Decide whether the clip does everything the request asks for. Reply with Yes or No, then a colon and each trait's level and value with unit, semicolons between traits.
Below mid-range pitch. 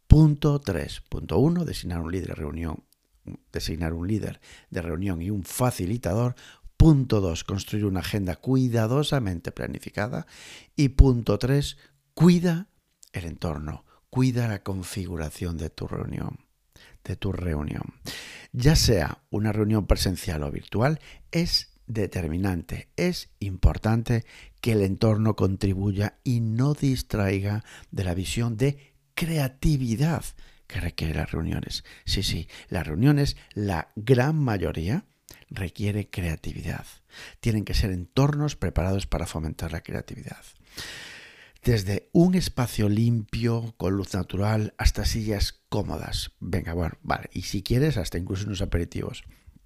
Yes: low, 105 Hz